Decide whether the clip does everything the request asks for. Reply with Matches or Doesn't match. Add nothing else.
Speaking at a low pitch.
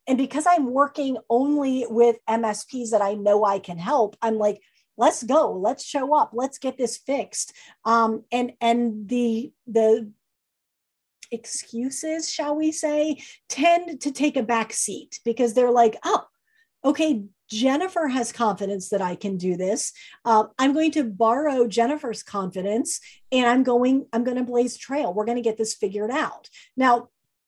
Doesn't match